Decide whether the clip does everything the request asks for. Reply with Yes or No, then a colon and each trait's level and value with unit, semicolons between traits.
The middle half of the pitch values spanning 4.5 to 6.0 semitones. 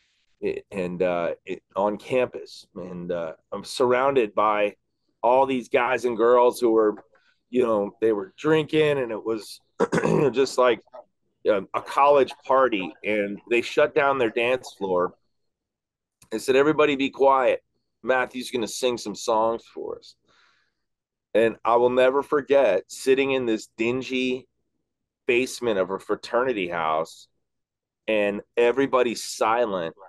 Yes: average, 4.8 semitones